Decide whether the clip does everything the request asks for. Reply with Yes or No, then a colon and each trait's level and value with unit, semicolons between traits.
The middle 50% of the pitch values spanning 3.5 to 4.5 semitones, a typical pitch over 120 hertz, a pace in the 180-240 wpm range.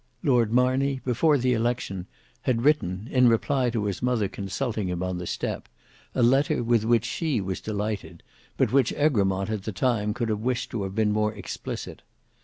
No: average, 3.8 semitones; low, 115 Hz; average, 185 wpm